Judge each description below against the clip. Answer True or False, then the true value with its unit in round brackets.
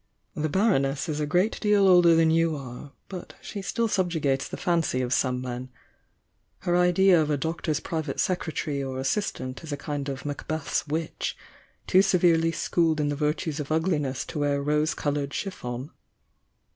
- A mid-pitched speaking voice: True (155 Hz)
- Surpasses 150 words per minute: True (170 wpm)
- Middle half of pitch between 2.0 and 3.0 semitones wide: False (3.8 semitones)